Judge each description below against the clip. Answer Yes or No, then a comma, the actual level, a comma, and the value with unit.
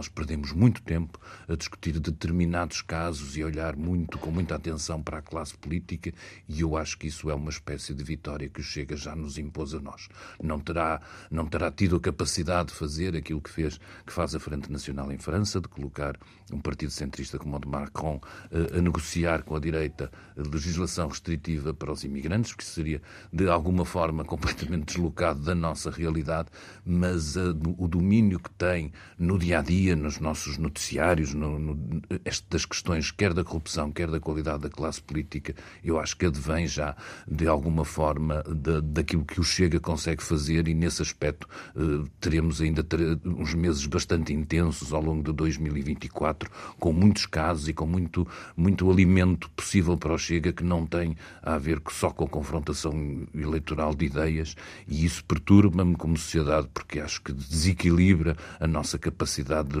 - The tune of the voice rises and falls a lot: No, narrow, 2.4 semitones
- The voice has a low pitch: Yes, very low, 80 Hz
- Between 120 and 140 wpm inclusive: No, average, 180 wpm